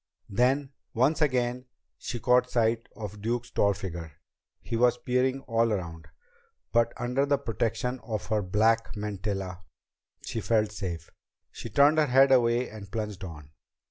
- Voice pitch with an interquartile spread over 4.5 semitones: No, average, 3.4 semitones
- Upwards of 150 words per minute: No, average, 145 wpm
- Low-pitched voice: Yes, low, 115 Hz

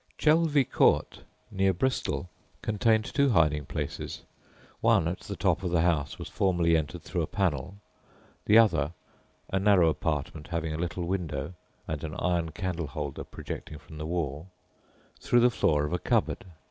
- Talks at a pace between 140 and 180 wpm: Yes, average, 160 wpm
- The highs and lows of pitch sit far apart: No, average, 4.1 semitones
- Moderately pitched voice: No, very low, 85 Hz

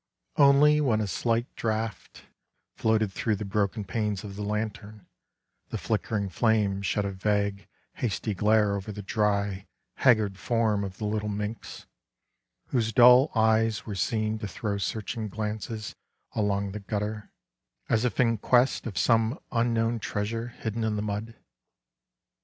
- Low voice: Yes, low, 110 Hz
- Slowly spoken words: No, average, 145 wpm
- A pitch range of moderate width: No, narrow, 1.9 semitones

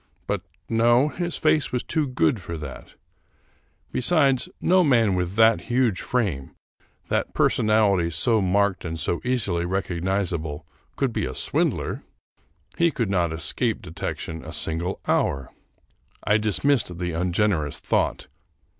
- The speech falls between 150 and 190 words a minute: No, slow, 135 wpm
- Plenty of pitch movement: Yes, wide, 6.4 semitones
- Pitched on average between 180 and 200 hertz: No, low, 100 Hz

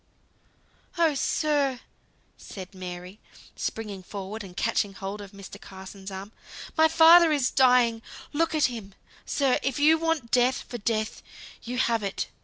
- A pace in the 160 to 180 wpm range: No, average, 145 wpm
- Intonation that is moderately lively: No, wide, 6.5 semitones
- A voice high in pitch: Yes, high, 230 Hz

